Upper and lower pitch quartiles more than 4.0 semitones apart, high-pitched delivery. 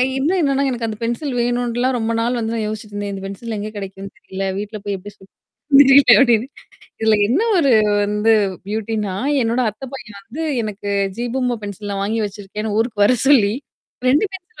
No: average, 3.3 semitones; high, 220 Hz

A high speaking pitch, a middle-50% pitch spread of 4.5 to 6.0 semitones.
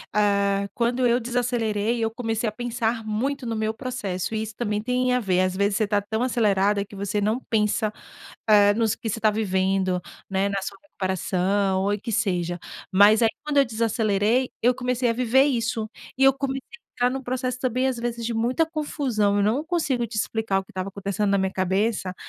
No: high, 220 Hz; average, 3.5 semitones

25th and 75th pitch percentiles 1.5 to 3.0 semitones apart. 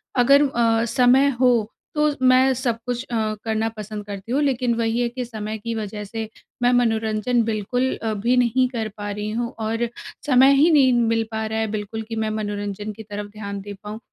Yes: narrow, 2.5 semitones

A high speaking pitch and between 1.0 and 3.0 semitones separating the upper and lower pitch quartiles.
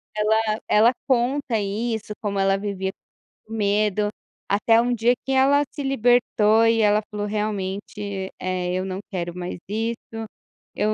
Yes: high, 210 Hz; narrow, 2.4 semitones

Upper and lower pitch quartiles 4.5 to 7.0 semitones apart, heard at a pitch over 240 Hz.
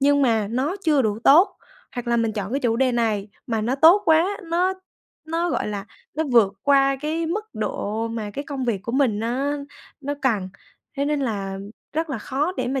Yes: average, 5.1 semitones; very high, 265 Hz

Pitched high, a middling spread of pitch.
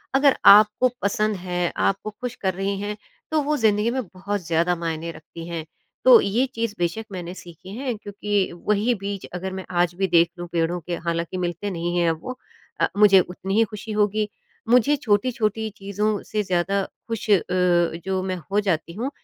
Yes: high, 195 Hz; average, 3.4 semitones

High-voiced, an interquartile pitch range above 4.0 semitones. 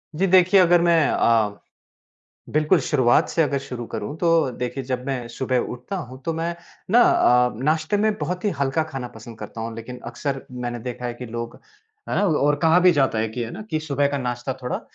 No: low, 135 Hz; average, 5.0 semitones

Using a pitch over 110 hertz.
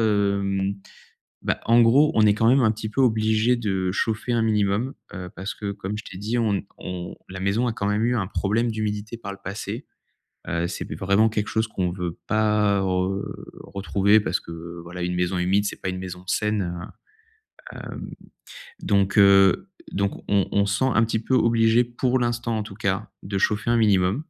No: low, 105 Hz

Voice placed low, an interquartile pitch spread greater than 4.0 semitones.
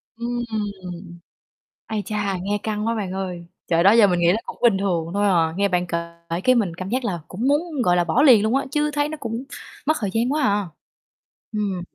No: high, 205 Hz; average, 4.8 semitones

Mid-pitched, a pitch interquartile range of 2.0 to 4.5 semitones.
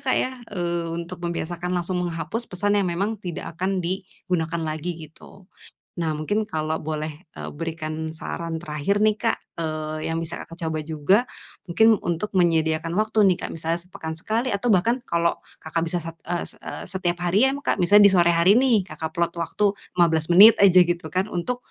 Yes: medium, 175 Hz; average, 3.1 semitones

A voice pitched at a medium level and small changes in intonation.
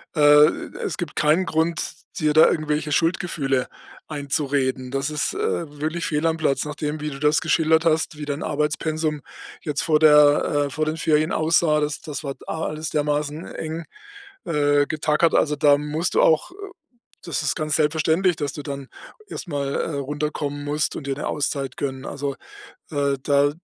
Yes: medium, 150 Hz; narrow, 1.5 semitones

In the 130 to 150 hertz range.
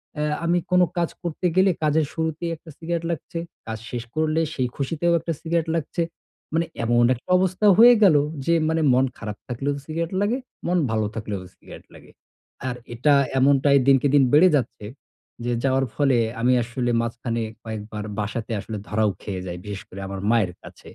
Yes: medium, 140 Hz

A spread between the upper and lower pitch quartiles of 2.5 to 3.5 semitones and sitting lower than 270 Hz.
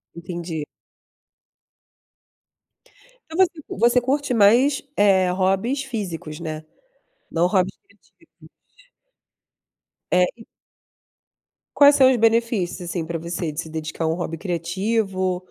No: wide, 5.6 semitones; high, 190 Hz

